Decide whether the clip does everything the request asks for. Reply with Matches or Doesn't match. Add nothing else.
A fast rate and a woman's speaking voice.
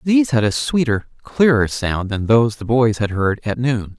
Doesn't match